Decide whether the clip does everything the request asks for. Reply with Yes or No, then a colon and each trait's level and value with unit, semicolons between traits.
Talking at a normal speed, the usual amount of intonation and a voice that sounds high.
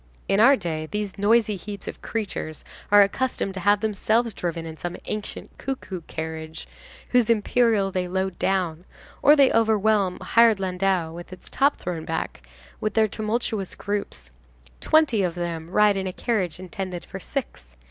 Yes: average, 165 wpm; average, 3.8 semitones; high, 195 Hz